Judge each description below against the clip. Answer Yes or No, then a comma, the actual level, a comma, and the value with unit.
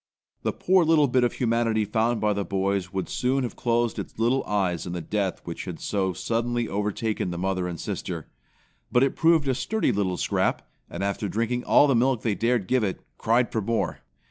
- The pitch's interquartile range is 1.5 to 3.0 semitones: No, average, 4.0 semitones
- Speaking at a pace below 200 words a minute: No, fast, 205 wpm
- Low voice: Yes, low, 110 Hz